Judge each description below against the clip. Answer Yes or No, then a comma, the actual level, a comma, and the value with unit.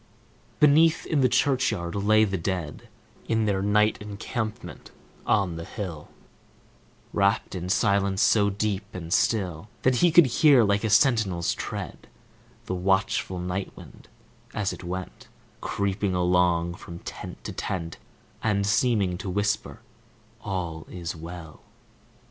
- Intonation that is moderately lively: Yes, average, 3.3 semitones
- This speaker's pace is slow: Yes, slow, 130 wpm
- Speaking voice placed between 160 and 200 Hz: No, low, 100 Hz